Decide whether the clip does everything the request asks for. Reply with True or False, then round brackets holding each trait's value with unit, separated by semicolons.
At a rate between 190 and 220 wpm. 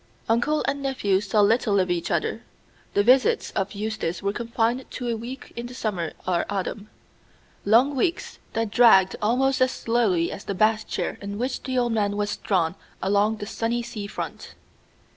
False (180 wpm)